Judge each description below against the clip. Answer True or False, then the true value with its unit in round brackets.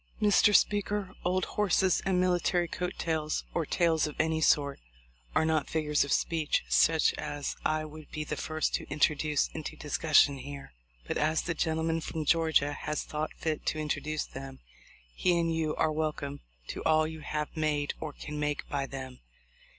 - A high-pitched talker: False (155 Hz)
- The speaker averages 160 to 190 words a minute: True (175 wpm)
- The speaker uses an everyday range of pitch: False (1.6 semitones)